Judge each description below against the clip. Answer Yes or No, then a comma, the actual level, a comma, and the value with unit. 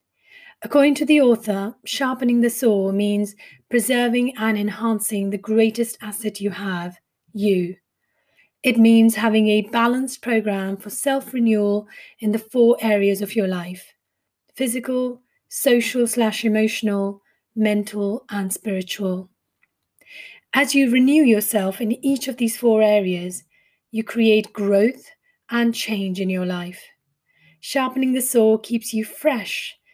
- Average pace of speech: No, slow, 125 wpm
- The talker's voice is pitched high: Yes, high, 220 Hz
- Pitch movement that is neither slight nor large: Yes, average, 3.4 semitones